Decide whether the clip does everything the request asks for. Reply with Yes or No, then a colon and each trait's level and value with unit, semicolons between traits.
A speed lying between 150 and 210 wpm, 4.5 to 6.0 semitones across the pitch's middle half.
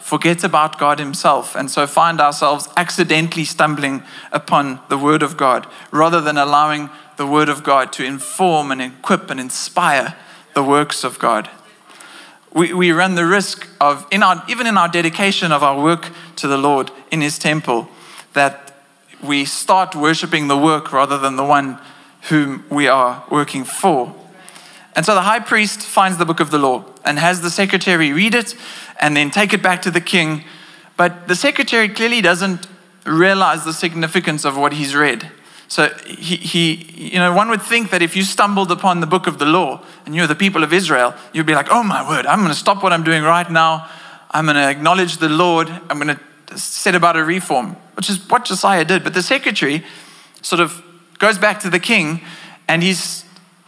No: average, 195 wpm; average, 3.9 semitones